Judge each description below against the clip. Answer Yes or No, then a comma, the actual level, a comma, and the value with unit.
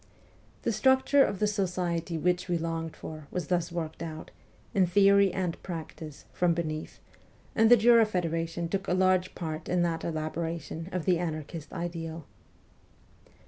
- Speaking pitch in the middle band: Yes, medium, 170 Hz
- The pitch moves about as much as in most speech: No, narrow, 2.3 semitones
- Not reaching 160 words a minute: Yes, average, 150 wpm